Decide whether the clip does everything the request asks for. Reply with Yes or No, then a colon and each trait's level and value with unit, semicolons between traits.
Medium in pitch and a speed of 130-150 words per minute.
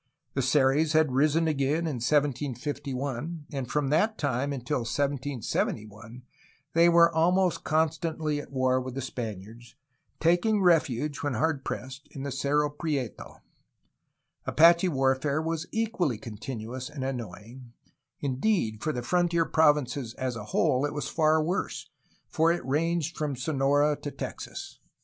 Yes: medium, 145 Hz; average, 140 wpm